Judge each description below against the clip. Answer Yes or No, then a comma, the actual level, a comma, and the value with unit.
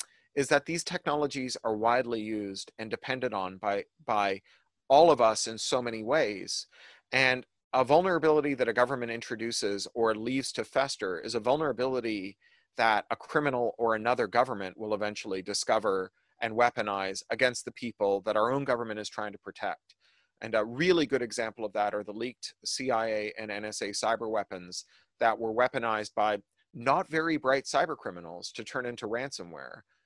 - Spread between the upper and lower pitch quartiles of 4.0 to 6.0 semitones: No, average, 3.6 semitones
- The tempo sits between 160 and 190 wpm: Yes, average, 165 wpm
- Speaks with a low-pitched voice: Yes, low, 115 Hz